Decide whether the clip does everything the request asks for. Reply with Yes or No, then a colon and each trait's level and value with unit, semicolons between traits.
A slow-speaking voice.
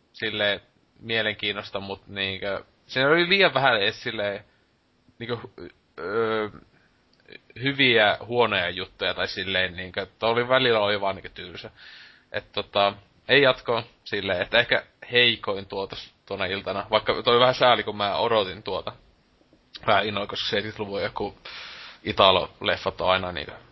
No: average, 125 wpm